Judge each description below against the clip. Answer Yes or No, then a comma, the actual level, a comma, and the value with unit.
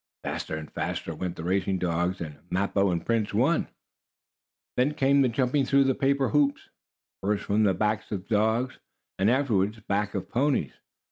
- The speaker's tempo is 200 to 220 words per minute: No, average, 175 wpm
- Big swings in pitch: Yes, wide, 5.7 semitones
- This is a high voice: No, low, 105 Hz